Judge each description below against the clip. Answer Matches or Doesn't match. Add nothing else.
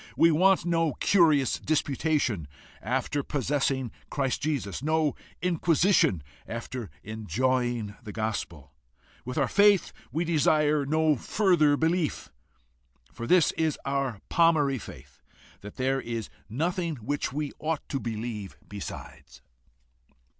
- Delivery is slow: Matches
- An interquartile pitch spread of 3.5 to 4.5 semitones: Doesn't match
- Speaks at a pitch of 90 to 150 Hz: Matches